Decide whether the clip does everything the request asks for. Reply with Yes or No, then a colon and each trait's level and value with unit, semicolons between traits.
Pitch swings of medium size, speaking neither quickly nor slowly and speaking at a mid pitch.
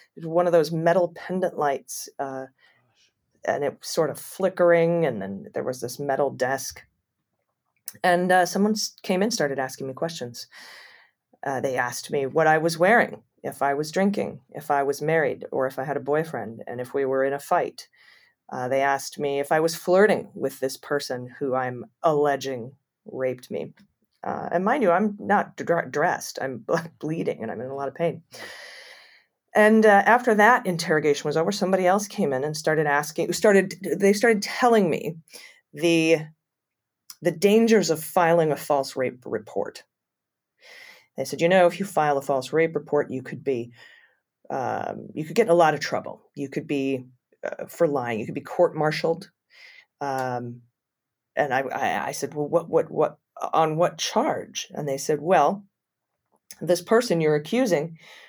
Yes: average, 4.8 semitones; average, 180 wpm; medium, 155 Hz